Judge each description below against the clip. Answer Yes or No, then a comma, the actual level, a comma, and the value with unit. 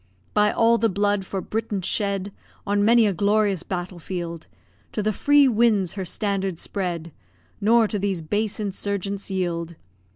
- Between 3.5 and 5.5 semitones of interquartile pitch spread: No, narrow, 2.4 semitones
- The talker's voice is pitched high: Yes, high, 200 Hz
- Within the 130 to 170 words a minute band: Yes, average, 155 wpm